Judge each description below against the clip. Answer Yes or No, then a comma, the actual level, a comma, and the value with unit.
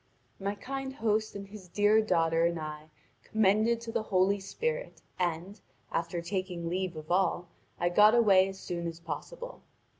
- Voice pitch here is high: Yes, high, 195 Hz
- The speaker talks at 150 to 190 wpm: Yes, average, 155 wpm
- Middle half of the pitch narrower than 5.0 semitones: Yes, average, 3.9 semitones